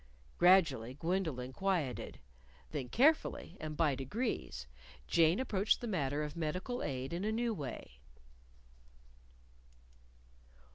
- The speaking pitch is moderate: Yes, medium, 165 Hz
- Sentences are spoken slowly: Yes, slow, 105 wpm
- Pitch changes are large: Yes, wide, 6.4 semitones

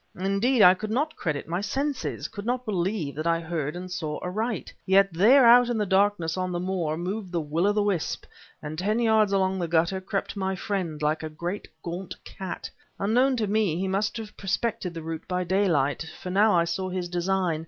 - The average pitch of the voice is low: No, high, 190 Hz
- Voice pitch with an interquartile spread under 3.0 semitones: No, average, 3.5 semitones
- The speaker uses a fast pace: Yes, fast, 210 wpm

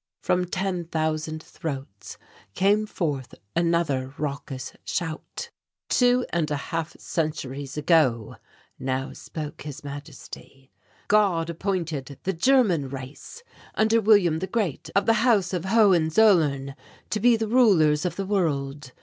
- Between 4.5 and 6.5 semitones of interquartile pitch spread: Yes, wide, 5.6 semitones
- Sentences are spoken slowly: Yes, slow, 125 wpm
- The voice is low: No, medium, 165 Hz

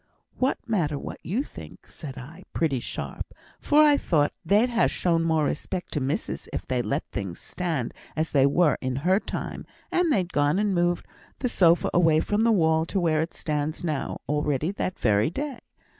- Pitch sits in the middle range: Yes, medium, 165 Hz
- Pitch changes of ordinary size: Yes, average, 4.8 semitones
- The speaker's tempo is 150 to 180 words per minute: No, average, 190 wpm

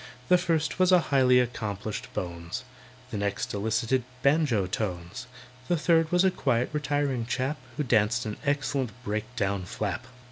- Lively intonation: Yes, wide, 5.8 semitones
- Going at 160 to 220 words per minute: No, average, 150 wpm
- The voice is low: Yes, low, 125 Hz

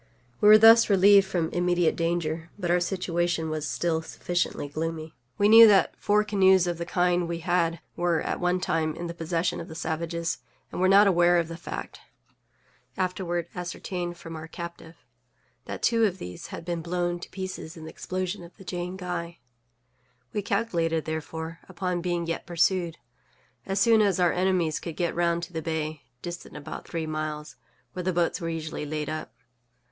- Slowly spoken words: No, average, 180 wpm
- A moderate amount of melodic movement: No, narrow, 2.0 semitones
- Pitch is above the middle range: No, medium, 175 Hz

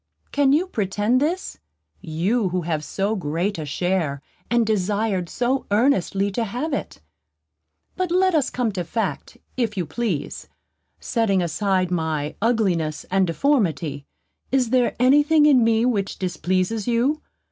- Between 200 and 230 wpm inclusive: No, average, 145 wpm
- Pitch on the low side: No, high, 210 Hz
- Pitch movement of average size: No, wide, 5.8 semitones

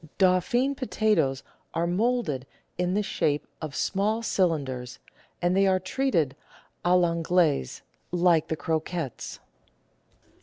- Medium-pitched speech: Yes, medium, 175 Hz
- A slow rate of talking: Yes, slow, 115 wpm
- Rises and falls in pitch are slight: No, average, 4.1 semitones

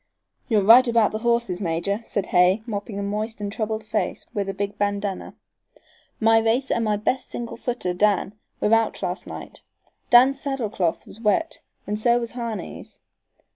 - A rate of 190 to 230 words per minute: No, average, 175 wpm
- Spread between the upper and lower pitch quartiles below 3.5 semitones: Yes, narrow, 2.6 semitones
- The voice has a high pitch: Yes, high, 215 Hz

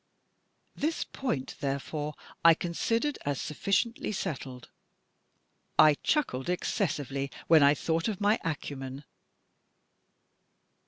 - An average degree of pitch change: No, wide, 6.2 semitones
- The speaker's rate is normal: No, slow, 100 wpm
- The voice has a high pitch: No, medium, 155 Hz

